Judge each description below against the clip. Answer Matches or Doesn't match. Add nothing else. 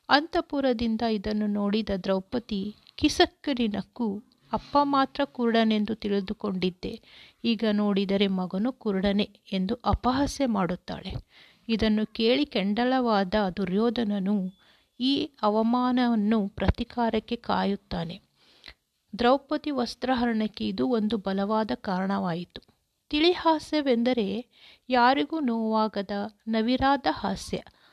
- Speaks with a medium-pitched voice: Doesn't match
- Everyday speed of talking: Matches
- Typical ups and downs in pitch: Matches